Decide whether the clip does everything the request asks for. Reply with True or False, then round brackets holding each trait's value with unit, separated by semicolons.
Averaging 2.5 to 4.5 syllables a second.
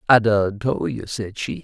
True (4.1 syllables/s)